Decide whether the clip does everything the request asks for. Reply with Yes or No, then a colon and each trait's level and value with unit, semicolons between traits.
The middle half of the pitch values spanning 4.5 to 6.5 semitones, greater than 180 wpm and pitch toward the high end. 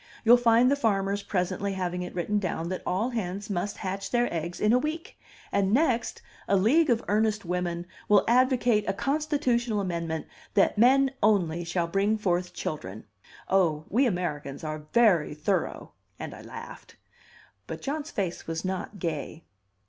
No: average, 5.1 semitones; average, 160 wpm; high, 195 Hz